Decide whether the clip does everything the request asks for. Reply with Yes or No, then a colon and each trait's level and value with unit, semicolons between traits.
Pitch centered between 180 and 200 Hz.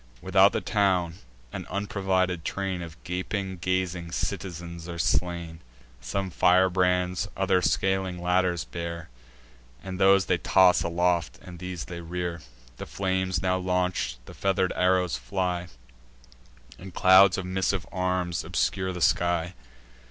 No: very low, 90 Hz